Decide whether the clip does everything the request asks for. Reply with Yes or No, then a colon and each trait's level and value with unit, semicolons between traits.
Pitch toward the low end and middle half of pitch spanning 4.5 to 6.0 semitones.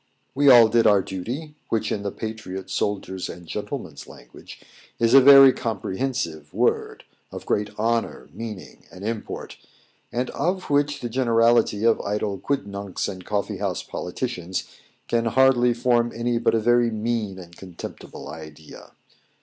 No: low, 115 Hz; average, 3.9 semitones